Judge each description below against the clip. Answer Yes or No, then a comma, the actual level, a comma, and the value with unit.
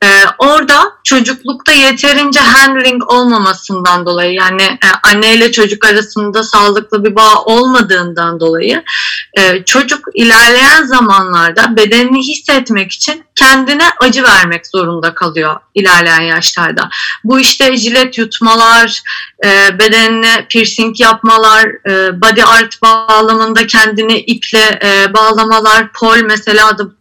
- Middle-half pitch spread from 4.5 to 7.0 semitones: No, average, 3.7 semitones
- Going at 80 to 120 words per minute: Yes, average, 110 wpm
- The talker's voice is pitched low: No, high, 225 Hz